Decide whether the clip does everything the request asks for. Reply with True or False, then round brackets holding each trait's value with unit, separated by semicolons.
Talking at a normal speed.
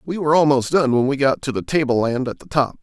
False (275 wpm)